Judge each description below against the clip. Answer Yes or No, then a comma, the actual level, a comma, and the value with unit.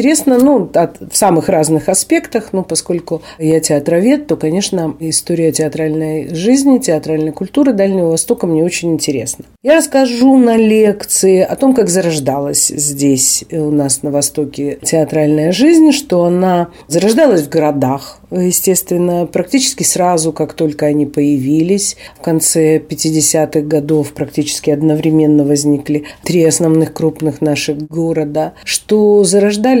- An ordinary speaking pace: Yes, average, 130 wpm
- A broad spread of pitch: No, average, 4.1 semitones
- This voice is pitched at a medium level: Yes, medium, 160 Hz